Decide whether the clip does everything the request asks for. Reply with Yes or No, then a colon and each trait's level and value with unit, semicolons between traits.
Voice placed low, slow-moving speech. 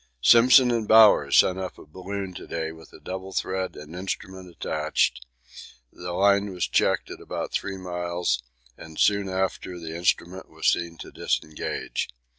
No: very low, 95 Hz; average, 160 wpm